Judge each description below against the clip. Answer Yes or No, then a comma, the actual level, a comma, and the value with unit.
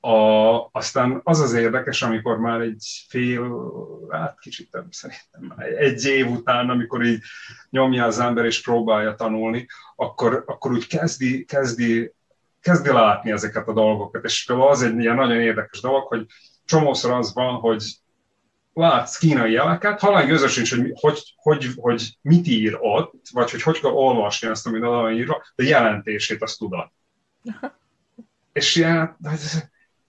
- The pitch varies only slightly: No, average, 3.6 semitones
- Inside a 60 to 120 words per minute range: No, average, 150 wpm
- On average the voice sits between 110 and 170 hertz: Yes, low, 120 Hz